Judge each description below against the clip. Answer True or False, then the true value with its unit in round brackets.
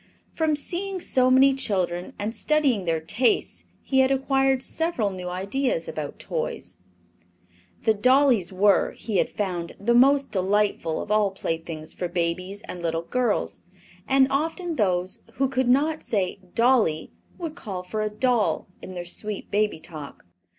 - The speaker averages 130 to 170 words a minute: True (150 wpm)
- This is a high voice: True (210 Hz)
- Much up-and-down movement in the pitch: True (6.7 semitones)